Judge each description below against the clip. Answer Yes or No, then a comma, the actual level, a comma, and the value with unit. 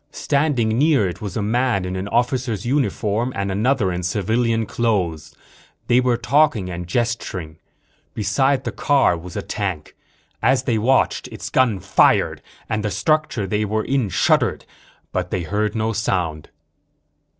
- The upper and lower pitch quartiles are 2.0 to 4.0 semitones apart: No, average, 4.8 semitones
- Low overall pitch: Yes, low, 110 Hz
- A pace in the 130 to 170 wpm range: Yes, average, 150 wpm